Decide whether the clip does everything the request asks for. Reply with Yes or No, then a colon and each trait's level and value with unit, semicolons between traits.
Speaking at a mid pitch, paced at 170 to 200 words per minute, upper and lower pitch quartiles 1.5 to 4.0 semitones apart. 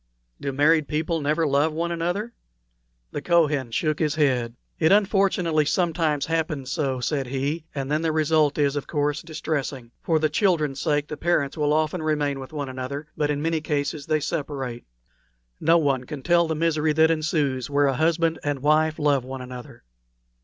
Yes: medium, 150 Hz; average, 180 wpm; narrow, 2.4 semitones